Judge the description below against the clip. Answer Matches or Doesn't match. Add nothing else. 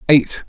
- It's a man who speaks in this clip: Matches